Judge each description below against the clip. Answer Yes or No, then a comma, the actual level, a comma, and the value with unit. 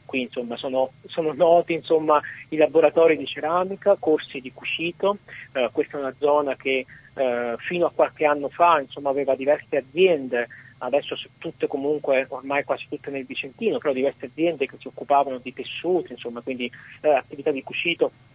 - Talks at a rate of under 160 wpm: No, average, 165 wpm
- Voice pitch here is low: No, medium, 145 Hz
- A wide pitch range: No, average, 3.5 semitones